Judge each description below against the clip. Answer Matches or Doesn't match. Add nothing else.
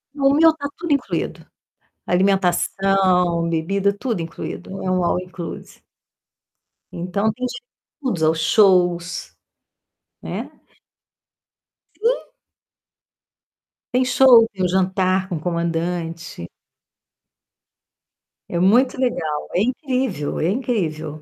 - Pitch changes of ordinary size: Doesn't match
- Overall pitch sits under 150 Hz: Doesn't match